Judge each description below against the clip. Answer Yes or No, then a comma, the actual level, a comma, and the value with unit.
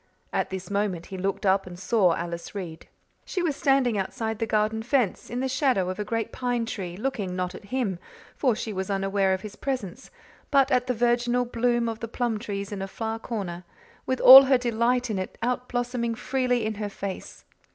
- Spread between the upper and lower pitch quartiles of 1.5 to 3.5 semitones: No, average, 4.2 semitones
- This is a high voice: Yes, high, 225 Hz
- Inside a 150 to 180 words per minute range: No, fast, 205 wpm